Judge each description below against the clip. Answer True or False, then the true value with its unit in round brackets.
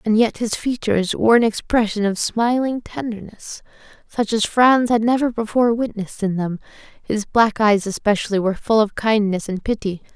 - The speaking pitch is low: False (220 Hz)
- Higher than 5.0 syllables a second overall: True (5.2 syllables/s)